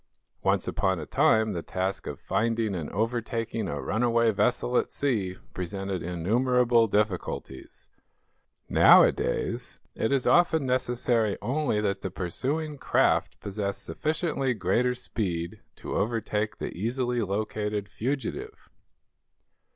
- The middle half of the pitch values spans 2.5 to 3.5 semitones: No, average, 4.2 semitones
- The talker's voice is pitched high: No, low, 110 Hz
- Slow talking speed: Yes, slow, 115 wpm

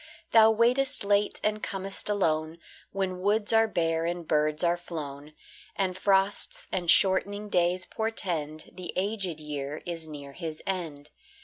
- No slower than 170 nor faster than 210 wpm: No, average, 140 wpm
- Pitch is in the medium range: Yes, medium, 180 Hz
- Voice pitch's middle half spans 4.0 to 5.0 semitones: Yes, average, 4.4 semitones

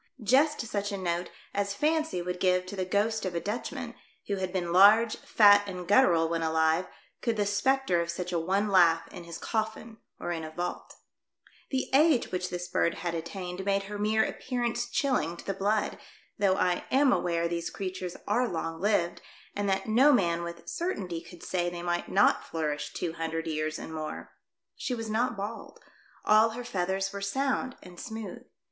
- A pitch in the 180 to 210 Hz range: Yes, high, 190 Hz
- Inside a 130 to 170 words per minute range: No, average, 190 wpm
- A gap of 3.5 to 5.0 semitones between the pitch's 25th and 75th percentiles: Yes, average, 4.1 semitones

